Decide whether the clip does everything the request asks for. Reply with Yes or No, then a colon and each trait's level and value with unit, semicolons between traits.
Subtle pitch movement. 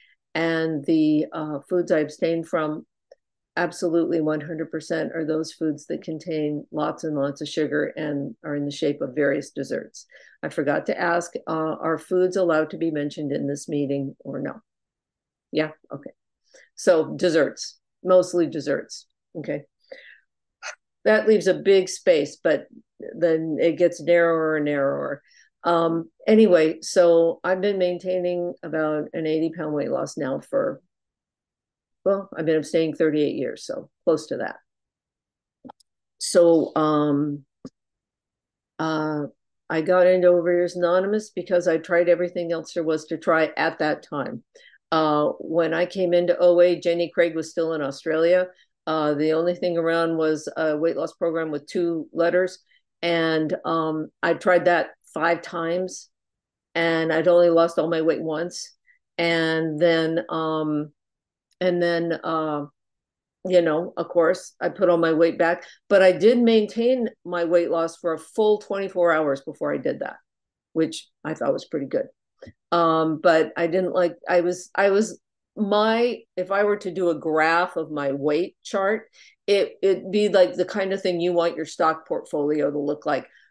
Yes: narrow, 2.3 semitones